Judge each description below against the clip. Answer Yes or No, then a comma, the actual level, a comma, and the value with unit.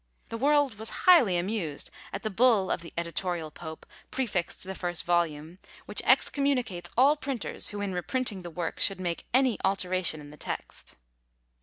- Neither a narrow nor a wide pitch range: No, wide, 5.7 semitones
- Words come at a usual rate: Yes, average, 170 wpm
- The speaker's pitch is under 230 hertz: Yes, high, 190 Hz